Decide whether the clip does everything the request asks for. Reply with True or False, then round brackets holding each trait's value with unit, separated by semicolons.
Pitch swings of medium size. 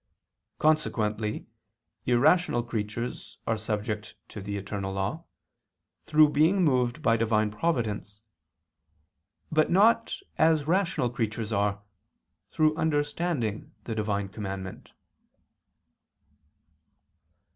False (6.7 semitones)